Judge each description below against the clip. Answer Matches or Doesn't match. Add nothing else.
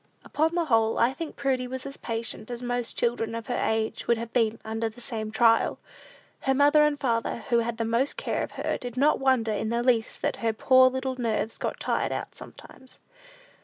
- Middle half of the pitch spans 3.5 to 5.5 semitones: Doesn't match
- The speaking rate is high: Matches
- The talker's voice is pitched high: Matches